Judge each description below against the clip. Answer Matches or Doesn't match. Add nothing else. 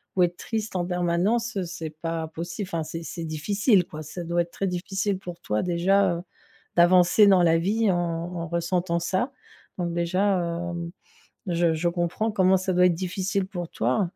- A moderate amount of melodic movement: Doesn't match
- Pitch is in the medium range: Matches